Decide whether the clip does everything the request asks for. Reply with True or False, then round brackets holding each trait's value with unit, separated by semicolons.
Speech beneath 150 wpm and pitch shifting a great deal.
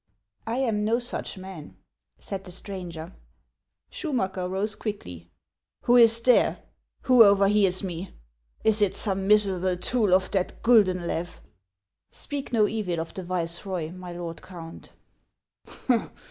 False (140 wpm; 3.3 semitones)